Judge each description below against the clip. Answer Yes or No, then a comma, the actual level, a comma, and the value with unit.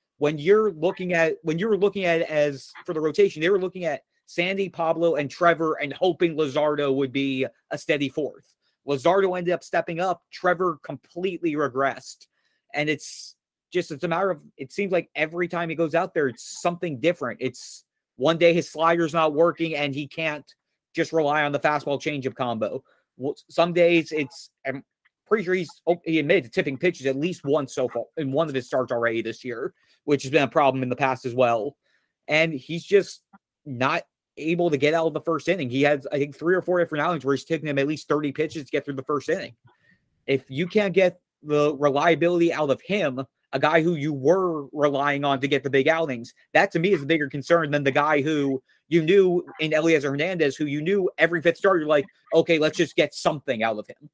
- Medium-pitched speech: Yes, medium, 155 Hz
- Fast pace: Yes, fast, 220 wpm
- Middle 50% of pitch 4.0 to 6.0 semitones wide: No, average, 3.3 semitones